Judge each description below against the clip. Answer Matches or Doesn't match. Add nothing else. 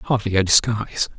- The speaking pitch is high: Doesn't match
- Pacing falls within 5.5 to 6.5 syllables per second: Matches